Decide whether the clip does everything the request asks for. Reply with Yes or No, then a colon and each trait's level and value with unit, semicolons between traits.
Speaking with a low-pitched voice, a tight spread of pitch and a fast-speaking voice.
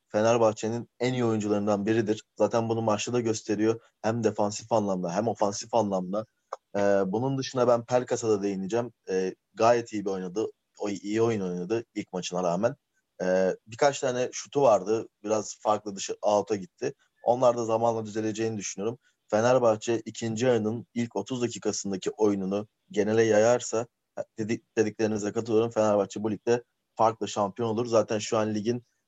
Yes: low, 110 Hz; narrow, 1.9 semitones; fast, 150 wpm